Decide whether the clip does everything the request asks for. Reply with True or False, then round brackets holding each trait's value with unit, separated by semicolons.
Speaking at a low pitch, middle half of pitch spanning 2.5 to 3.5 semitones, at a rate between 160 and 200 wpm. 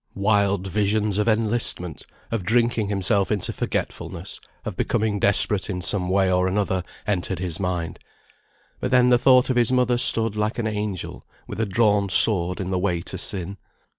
True (100 Hz; 3.0 semitones; 170 wpm)